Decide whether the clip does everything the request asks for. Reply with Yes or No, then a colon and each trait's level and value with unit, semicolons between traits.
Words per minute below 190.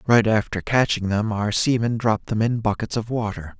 No: average, 200 wpm